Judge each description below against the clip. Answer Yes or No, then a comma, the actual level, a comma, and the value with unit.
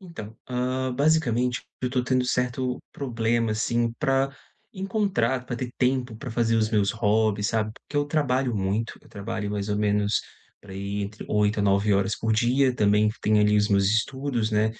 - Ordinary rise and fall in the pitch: Yes, average, 3.5 semitones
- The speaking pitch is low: Yes, low, 115 Hz